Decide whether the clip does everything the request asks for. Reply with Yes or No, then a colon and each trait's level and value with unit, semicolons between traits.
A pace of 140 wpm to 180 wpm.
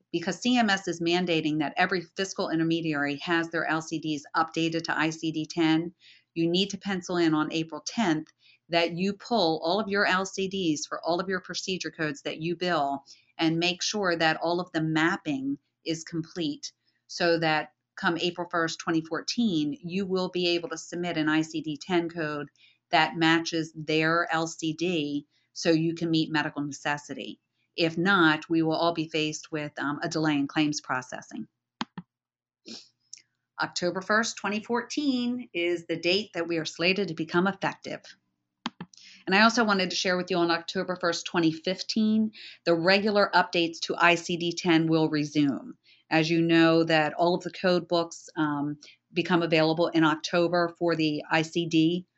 Yes: average, 160 wpm